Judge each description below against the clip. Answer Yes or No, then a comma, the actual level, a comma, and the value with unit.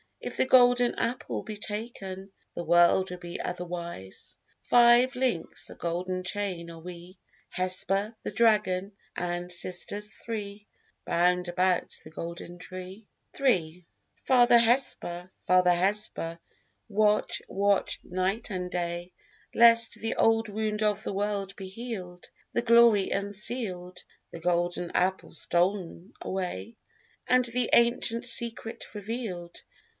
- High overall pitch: Yes, high, 195 Hz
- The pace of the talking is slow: Yes, slow, 120 wpm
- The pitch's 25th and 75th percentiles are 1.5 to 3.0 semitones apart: No, average, 4.1 semitones